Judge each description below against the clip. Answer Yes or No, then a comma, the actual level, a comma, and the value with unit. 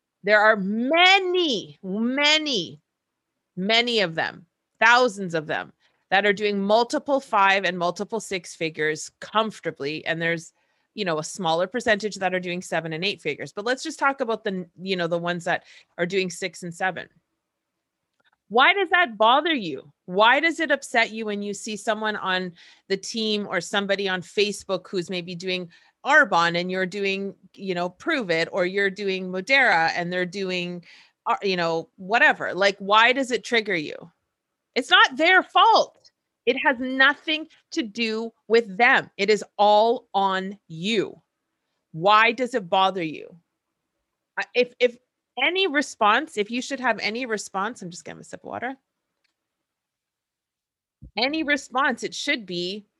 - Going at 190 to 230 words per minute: No, average, 160 wpm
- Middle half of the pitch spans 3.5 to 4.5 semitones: No, average, 5.0 semitones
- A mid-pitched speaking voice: No, high, 205 Hz